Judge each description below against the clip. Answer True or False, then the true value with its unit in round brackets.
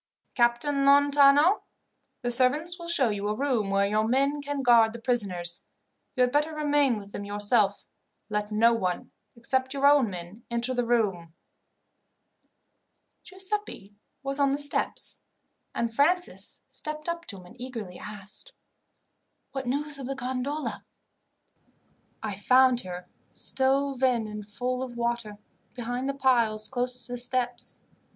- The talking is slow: False (145 wpm)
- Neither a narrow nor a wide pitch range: True (4.6 semitones)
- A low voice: False (245 Hz)